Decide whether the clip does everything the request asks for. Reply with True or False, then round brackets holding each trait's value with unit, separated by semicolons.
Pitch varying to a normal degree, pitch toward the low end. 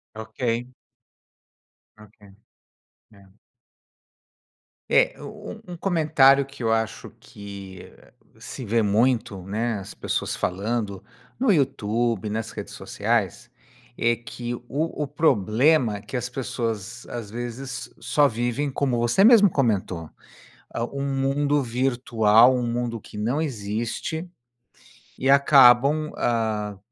True (3.9 semitones; 120 Hz)